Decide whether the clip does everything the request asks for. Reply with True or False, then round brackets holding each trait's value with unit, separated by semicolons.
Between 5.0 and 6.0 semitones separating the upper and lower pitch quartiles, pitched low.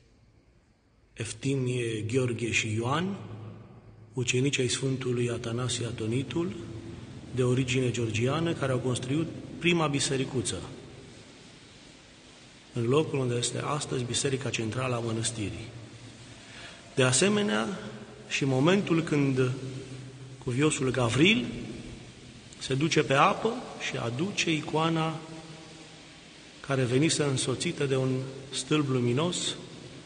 False (4.3 semitones; 130 Hz)